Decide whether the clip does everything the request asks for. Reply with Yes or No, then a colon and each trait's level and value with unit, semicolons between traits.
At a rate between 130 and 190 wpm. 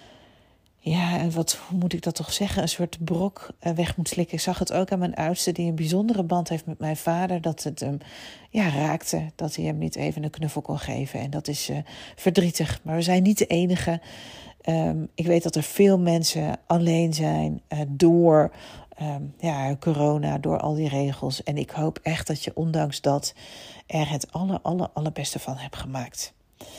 No: fast, 200 wpm